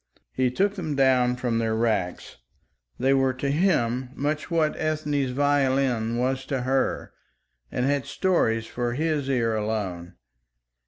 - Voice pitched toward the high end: No, low, 130 Hz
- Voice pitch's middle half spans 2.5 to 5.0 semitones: Yes, average, 3.4 semitones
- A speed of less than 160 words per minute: Yes, average, 140 wpm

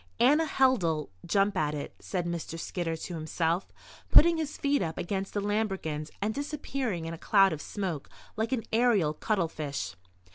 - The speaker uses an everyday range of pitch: No, wide, 5.8 semitones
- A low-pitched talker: No, high, 190 Hz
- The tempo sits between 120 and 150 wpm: No, average, 160 wpm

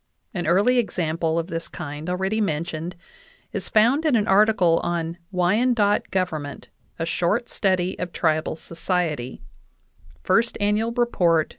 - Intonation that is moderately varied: Yes, average, 4.2 semitones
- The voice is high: No, medium, 180 Hz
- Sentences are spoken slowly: Yes, slow, 130 wpm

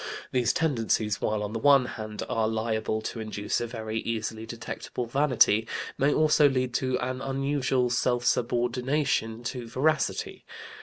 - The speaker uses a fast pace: No, average, 150 wpm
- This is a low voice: Yes, low, 120 Hz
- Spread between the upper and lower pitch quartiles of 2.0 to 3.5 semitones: Yes, average, 3.0 semitones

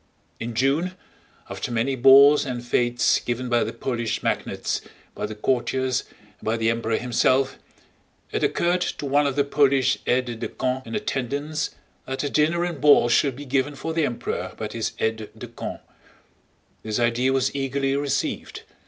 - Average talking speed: Yes, average, 170 wpm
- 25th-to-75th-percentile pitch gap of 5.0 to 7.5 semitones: No, average, 3.0 semitones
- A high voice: No, low, 130 Hz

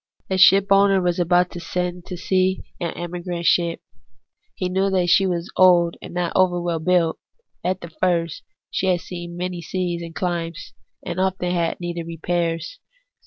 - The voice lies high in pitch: No, medium, 175 Hz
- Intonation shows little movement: Yes, narrow, 1.4 semitones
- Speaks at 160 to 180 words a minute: Yes, average, 170 wpm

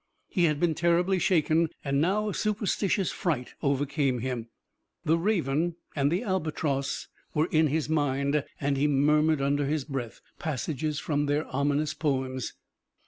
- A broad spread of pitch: No, average, 3.2 semitones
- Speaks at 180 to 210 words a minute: No, average, 145 wpm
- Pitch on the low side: No, medium, 150 Hz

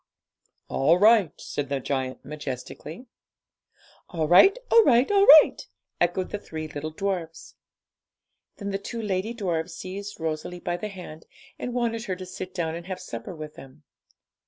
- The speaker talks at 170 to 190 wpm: No, average, 160 wpm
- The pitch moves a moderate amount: Yes, average, 4.6 semitones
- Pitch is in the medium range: Yes, medium, 180 Hz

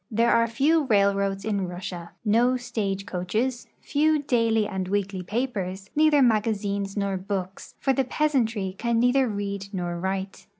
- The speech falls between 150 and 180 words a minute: Yes, average, 155 wpm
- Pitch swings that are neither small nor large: Yes, average, 3.9 semitones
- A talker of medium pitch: No, high, 210 Hz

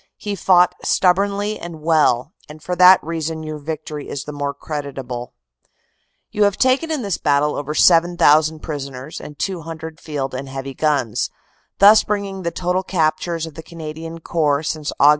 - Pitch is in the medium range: Yes, medium, 160 Hz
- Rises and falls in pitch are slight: No, average, 3.5 semitones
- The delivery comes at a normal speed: Yes, average, 160 wpm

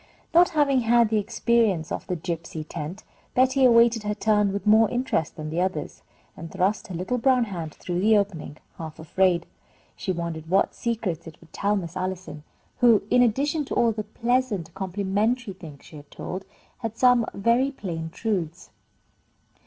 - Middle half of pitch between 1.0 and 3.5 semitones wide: No, wide, 5.6 semitones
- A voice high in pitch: Yes, high, 200 Hz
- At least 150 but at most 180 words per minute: Yes, average, 175 wpm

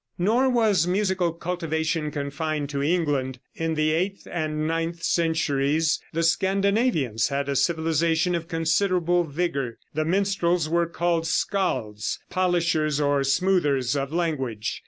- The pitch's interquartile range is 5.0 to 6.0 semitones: No, average, 3.2 semitones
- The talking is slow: Yes, slow, 125 wpm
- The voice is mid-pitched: Yes, medium, 165 Hz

